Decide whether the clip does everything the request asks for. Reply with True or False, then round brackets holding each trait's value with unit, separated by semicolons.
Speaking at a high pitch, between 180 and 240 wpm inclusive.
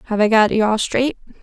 False (220 Hz; 250 wpm)